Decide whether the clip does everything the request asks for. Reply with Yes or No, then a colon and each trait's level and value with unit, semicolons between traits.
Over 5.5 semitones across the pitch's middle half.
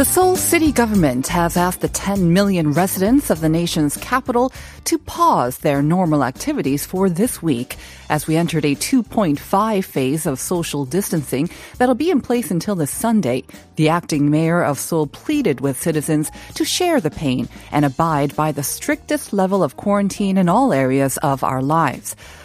Yes: wide, 6.2 semitones